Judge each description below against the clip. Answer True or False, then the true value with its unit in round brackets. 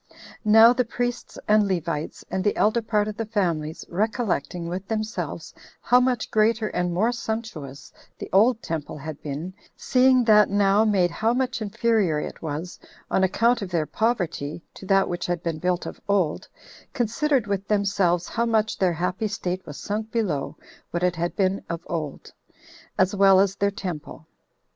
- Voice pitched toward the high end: True (195 Hz)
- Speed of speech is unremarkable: True (170 wpm)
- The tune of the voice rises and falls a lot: False (4.2 semitones)